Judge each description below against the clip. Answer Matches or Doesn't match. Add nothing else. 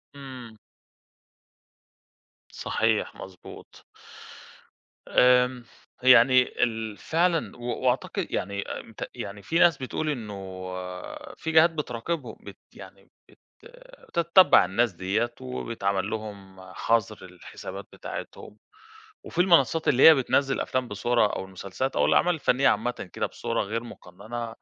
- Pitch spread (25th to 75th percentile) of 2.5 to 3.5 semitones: Doesn't match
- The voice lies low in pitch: Matches